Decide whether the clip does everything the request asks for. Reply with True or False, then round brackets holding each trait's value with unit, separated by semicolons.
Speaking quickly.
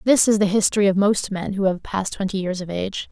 True (270 wpm)